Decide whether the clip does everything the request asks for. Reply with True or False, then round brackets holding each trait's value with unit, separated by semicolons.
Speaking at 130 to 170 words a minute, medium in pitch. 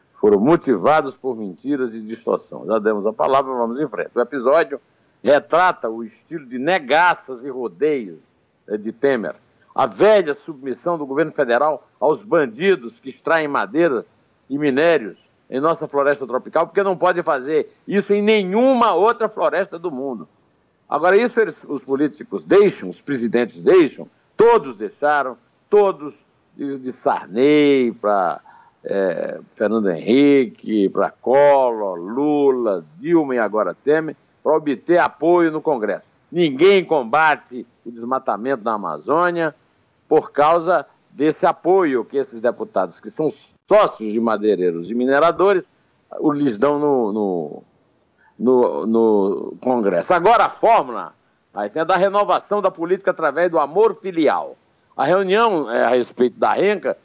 True (135 wpm; 145 Hz)